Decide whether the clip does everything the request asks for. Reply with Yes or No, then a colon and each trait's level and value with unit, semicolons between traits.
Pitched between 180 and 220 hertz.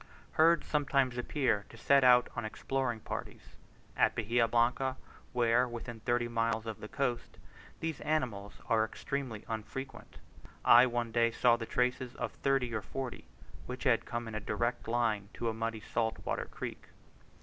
No: low, 120 Hz